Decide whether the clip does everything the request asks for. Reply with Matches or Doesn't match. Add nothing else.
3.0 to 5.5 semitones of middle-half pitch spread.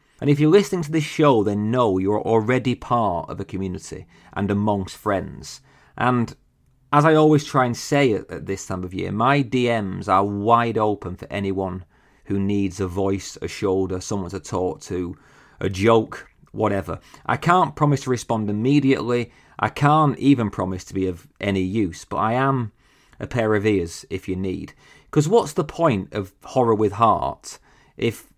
Matches